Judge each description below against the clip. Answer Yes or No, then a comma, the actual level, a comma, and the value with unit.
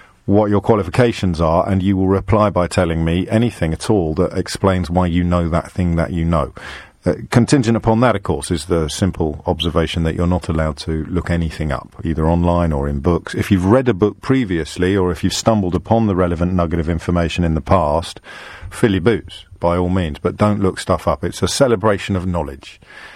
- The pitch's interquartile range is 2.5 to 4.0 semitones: Yes, average, 2.9 semitones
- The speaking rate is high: Yes, fast, 210 wpm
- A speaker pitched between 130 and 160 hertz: No, very low, 90 Hz